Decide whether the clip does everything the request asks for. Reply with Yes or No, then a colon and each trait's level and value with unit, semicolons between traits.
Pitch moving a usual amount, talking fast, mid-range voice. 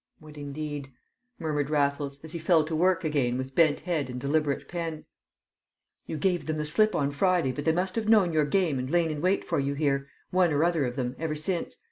Yes: average, 3.3 semitones; fast, 220 wpm; medium, 155 Hz